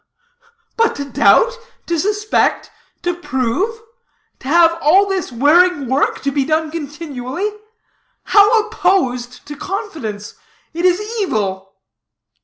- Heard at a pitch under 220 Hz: No, very high, 330 Hz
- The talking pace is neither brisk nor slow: No, slow, 115 wpm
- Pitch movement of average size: No, wide, 7.0 semitones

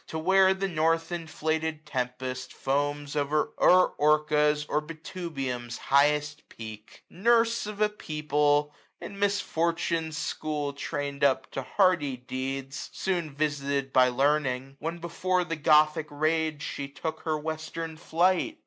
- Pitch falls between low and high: Yes, medium, 150 Hz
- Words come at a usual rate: No, slow, 130 wpm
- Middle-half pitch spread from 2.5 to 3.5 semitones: Yes, average, 2.8 semitones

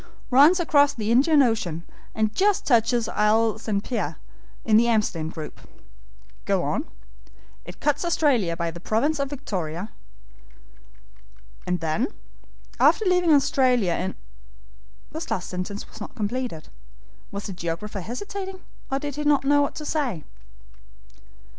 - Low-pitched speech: No, high, 230 Hz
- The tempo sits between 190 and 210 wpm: No, slow, 135 wpm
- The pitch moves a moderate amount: No, wide, 7.8 semitones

